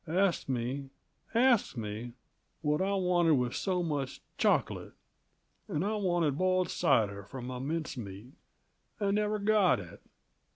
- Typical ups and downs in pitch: No, wide, 7.2 semitones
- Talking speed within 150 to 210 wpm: No, slow, 135 wpm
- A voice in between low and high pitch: Yes, medium, 155 Hz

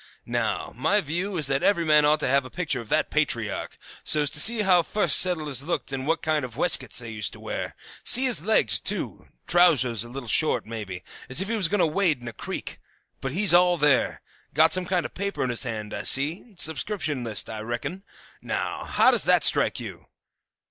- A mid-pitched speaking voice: Yes, medium, 150 Hz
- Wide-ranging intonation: Yes, wide, 6.0 semitones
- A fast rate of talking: Yes, fast, 220 wpm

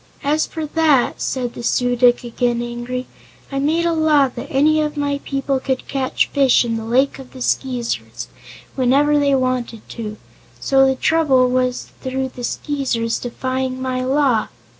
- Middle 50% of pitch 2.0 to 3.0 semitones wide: Yes, narrow, 2.4 semitones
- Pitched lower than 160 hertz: No, very high, 260 Hz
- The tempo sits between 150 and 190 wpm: Yes, average, 165 wpm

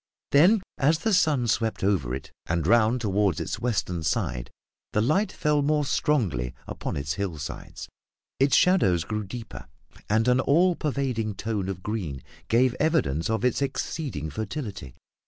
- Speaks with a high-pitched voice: No, low, 115 Hz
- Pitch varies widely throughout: Yes, wide, 7.4 semitones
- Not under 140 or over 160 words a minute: Yes, average, 150 wpm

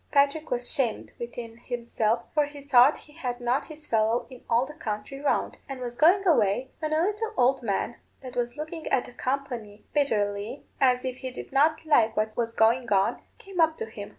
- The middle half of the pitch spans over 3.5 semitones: Yes, average, 4.2 semitones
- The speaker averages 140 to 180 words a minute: No, fast, 205 wpm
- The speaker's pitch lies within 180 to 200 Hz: No, very high, 255 Hz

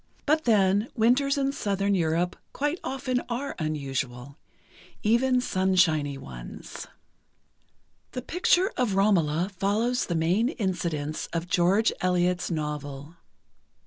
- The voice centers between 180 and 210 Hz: Yes, high, 190 Hz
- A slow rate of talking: Yes, slow, 110 wpm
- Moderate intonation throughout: No, wide, 7.2 semitones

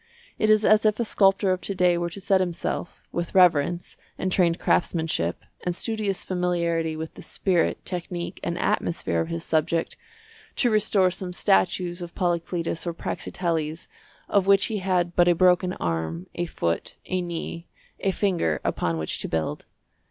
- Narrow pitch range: Yes, narrow, 2.2 semitones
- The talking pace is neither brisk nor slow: Yes, average, 165 wpm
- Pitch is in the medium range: Yes, medium, 175 Hz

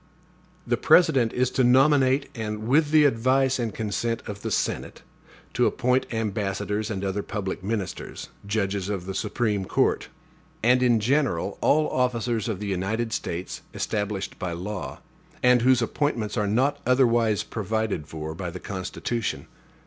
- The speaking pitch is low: Yes, low, 110 Hz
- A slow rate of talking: No, average, 150 wpm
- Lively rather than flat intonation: No, average, 3.9 semitones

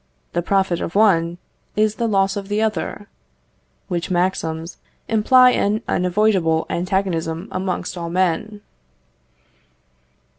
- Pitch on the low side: No, high, 190 Hz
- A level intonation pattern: No, average, 3.5 semitones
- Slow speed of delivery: Yes, slow, 110 wpm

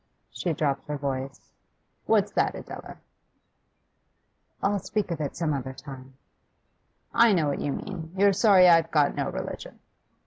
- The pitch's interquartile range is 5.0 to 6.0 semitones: Yes, wide, 5.4 semitones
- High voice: No, medium, 160 Hz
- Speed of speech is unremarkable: Yes, average, 145 wpm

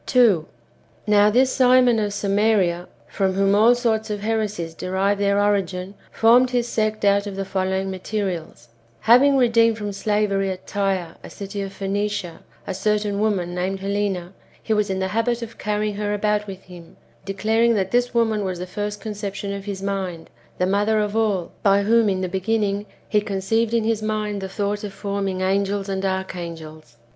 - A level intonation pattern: Yes, narrow, 2.1 semitones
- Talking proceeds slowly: No, average, 185 wpm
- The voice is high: Yes, high, 200 Hz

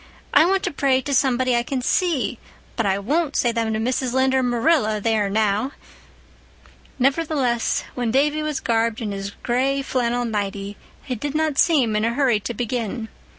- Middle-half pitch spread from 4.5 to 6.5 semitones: No, average, 3.8 semitones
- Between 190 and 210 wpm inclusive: No, average, 180 wpm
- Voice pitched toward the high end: Yes, high, 245 Hz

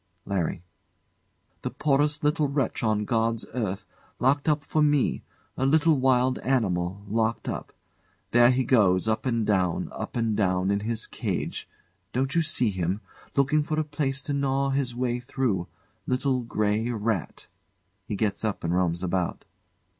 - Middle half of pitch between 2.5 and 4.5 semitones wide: No, average, 5.1 semitones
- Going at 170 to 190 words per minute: No, average, 155 wpm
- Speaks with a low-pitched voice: Yes, low, 120 Hz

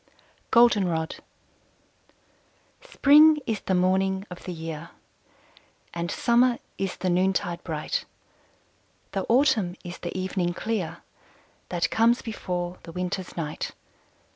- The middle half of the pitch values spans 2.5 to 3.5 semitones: No, average, 4.3 semitones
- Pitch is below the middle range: No, medium, 185 Hz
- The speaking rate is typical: No, slow, 110 wpm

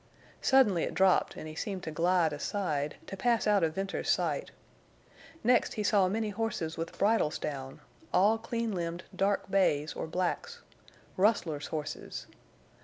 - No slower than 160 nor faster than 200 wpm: No, average, 140 wpm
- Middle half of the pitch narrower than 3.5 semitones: No, average, 4.7 semitones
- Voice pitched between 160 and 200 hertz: Yes, medium, 185 Hz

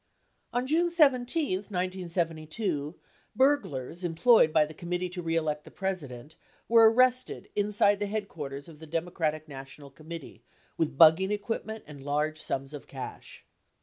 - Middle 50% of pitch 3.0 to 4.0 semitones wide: No, wide, 5.6 semitones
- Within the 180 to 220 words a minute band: No, average, 140 wpm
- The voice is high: No, medium, 170 Hz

